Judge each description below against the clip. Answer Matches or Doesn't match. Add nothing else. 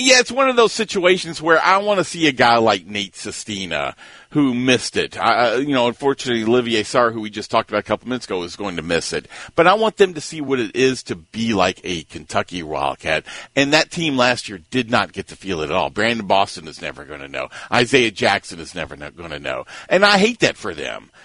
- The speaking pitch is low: Matches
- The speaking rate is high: Matches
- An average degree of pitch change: Doesn't match